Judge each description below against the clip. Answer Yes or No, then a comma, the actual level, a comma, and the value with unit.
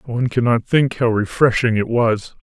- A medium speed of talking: Yes, average, 175 wpm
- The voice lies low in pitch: Yes, low, 120 Hz